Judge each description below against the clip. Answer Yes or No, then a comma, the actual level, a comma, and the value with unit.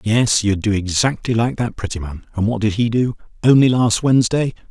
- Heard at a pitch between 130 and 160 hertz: No, low, 115 Hz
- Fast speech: No, average, 190 wpm